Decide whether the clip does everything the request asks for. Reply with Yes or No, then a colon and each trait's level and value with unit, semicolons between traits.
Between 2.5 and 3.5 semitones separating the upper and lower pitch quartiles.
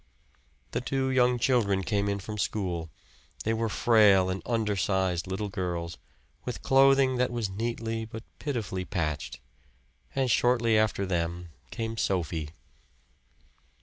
No: average, 4.0 semitones